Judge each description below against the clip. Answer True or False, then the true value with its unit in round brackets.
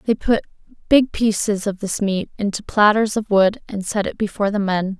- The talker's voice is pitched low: False (205 Hz)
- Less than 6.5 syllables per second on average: True (5.2 syllables/s)